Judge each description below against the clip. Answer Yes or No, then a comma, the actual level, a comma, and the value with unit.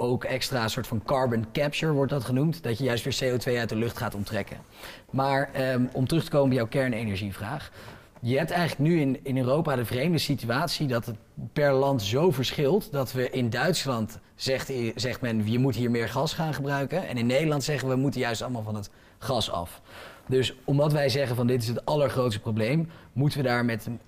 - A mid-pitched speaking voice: No, low, 130 Hz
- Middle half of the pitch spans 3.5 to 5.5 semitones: No, average, 3.1 semitones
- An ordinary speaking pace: No, fast, 210 wpm